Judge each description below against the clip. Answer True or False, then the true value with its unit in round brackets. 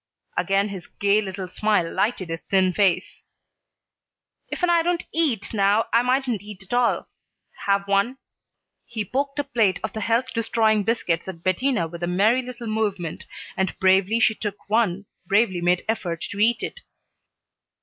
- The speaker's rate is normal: True (160 wpm)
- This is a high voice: True (210 Hz)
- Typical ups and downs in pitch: True (3.7 semitones)